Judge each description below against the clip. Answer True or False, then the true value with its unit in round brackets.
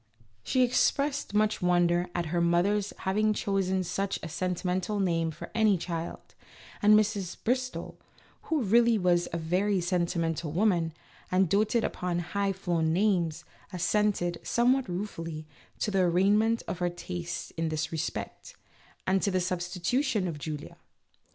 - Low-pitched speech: False (185 Hz)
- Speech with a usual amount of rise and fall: True (3.4 semitones)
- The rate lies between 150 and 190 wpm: False (140 wpm)